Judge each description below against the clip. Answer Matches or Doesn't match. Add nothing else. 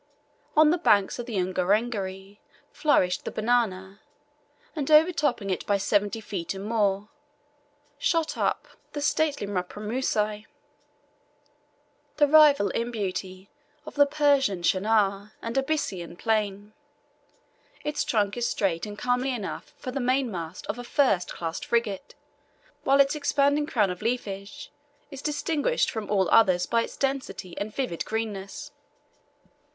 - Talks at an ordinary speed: Doesn't match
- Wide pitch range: Matches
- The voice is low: Doesn't match